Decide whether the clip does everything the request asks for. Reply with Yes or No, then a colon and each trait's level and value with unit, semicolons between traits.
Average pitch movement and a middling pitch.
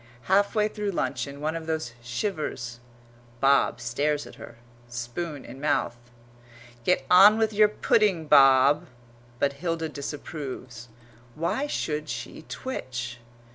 No: wide, 5.8 semitones; medium, 150 Hz